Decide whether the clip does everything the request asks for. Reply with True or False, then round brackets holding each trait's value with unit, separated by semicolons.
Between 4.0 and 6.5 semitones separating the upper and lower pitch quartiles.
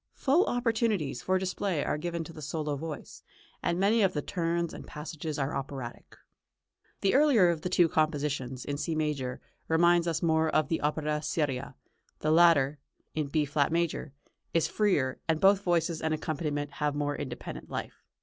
False (2.9 semitones)